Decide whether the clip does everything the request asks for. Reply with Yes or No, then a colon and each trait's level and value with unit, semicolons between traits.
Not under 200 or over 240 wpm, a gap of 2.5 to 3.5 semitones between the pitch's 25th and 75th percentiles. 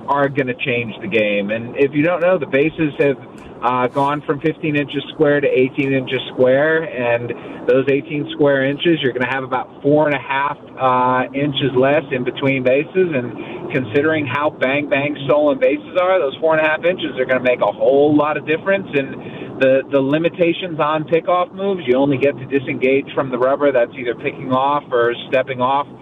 Yes: fast, 205 wpm; average, 3.1 semitones